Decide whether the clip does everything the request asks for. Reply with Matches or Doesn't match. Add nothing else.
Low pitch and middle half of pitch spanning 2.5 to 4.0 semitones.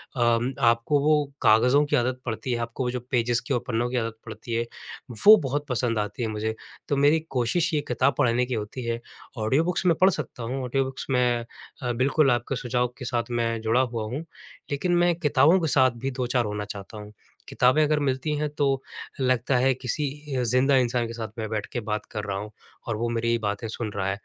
Matches